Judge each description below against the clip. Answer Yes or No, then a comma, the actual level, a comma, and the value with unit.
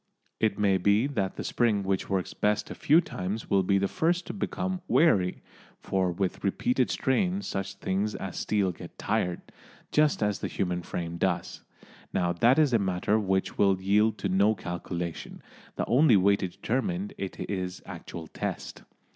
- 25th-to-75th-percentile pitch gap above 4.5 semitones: No, average, 3.9 semitones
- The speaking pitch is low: Yes, low, 100 Hz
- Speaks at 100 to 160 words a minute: No, average, 170 wpm